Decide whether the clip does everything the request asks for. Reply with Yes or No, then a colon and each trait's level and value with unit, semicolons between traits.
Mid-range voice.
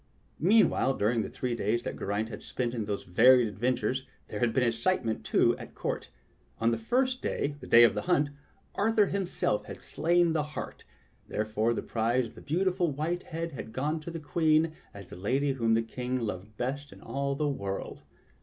No: low, 130 Hz